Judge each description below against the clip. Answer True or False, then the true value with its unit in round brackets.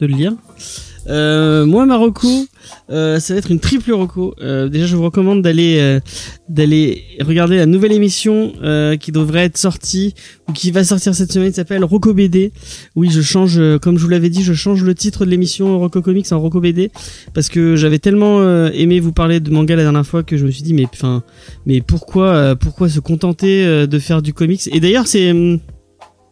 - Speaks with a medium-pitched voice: True (170 Hz)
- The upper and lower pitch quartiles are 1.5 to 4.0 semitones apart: True (3.6 semitones)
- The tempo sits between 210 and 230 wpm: True (215 wpm)